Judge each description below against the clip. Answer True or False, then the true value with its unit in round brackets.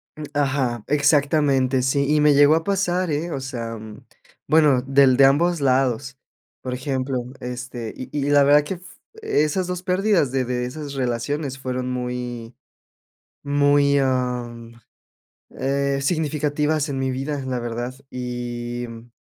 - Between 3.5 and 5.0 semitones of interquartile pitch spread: False (2.9 semitones)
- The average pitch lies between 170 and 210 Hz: False (135 Hz)